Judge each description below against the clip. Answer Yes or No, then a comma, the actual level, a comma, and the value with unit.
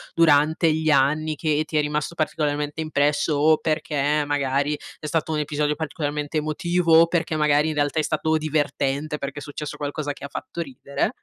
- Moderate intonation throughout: No, narrow, 1.4 semitones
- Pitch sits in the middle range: Yes, medium, 150 Hz